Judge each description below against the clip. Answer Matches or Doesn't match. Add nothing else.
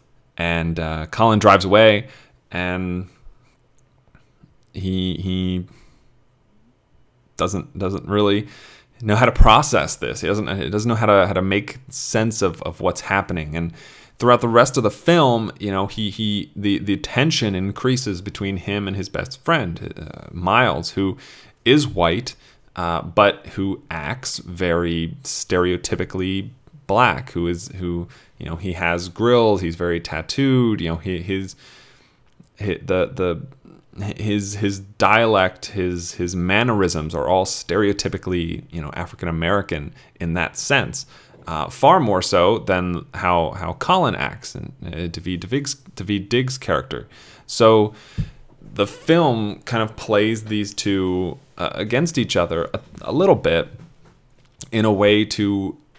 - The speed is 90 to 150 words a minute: Matches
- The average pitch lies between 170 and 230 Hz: Doesn't match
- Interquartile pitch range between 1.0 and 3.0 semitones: Doesn't match